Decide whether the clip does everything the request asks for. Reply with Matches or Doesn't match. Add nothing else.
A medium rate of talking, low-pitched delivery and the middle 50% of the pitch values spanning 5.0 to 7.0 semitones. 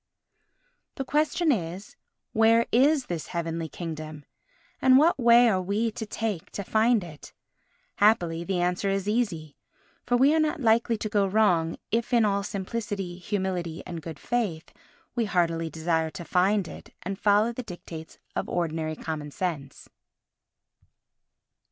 Doesn't match